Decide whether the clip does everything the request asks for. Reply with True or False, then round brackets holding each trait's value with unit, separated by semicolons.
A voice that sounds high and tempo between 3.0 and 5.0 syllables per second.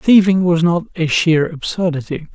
False (170 Hz; 4.6 syllables/s)